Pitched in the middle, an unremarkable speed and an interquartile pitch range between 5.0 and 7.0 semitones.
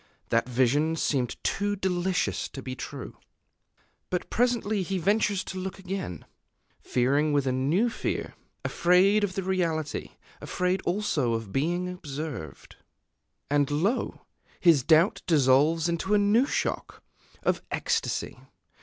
No: medium, 170 Hz; slow, 125 wpm; wide, 5.4 semitones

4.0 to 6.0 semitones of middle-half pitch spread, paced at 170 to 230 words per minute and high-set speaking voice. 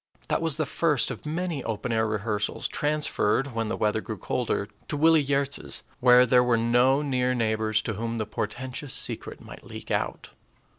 No: average, 4.3 semitones; average, 180 wpm; low, 125 Hz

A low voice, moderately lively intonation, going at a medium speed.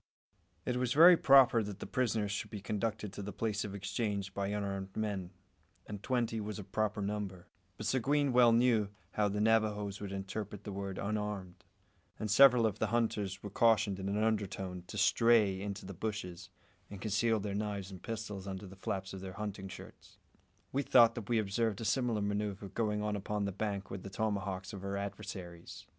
No: low, 105 Hz; narrow, 2.1 semitones; average, 195 wpm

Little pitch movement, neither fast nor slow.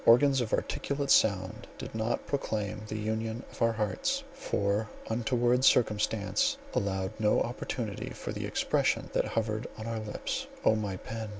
Yes: narrow, 2.3 semitones; average, 155 wpm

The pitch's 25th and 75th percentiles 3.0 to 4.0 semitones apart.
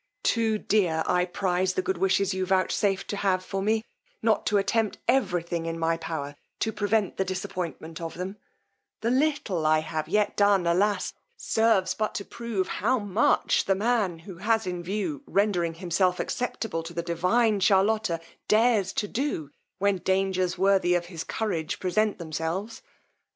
Yes: average, 3.6 semitones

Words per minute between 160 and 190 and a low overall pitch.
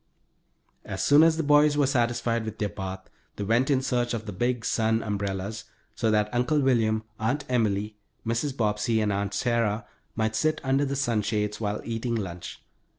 Yes: average, 175 wpm; low, 115 Hz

